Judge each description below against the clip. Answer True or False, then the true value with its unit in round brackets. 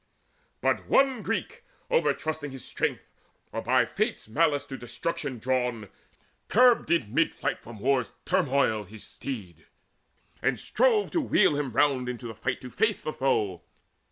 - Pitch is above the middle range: False (135 Hz)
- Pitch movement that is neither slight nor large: False (6.0 semitones)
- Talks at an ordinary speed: True (155 wpm)